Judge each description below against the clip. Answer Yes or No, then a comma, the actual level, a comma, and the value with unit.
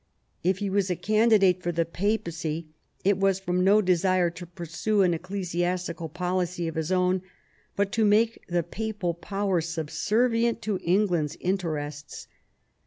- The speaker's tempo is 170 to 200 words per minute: No, average, 155 wpm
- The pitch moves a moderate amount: Yes, average, 3.0 semitones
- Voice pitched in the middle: Yes, medium, 180 Hz